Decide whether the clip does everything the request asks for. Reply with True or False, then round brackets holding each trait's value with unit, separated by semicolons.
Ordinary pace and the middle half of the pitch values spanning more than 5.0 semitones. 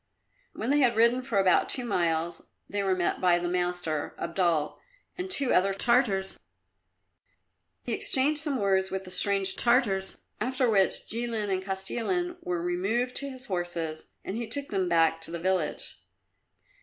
True (160 wpm; 5.4 semitones)